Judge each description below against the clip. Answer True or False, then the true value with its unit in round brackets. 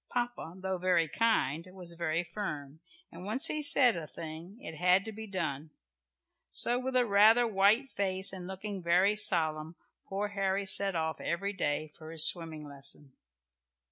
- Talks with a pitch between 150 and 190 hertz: True (185 Hz)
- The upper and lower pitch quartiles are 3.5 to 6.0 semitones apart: True (4.3 semitones)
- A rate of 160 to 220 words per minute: True (165 wpm)